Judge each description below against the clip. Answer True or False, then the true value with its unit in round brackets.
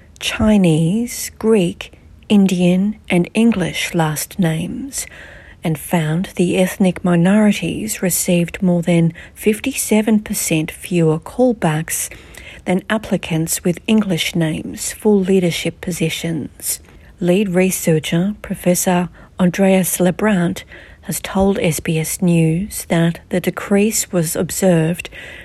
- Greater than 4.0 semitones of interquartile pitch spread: False (3.2 semitones)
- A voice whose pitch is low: False (180 Hz)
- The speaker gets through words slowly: True (95 wpm)